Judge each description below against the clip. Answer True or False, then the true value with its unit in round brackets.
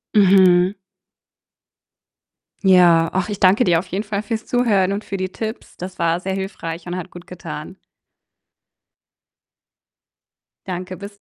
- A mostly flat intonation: True (2.1 semitones)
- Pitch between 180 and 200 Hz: True (185 Hz)